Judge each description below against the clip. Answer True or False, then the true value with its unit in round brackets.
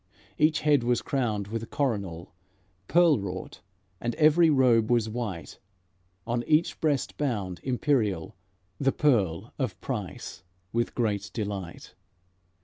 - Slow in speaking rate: True (120 wpm)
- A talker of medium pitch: False (120 Hz)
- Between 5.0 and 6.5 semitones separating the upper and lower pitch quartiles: True (5.6 semitones)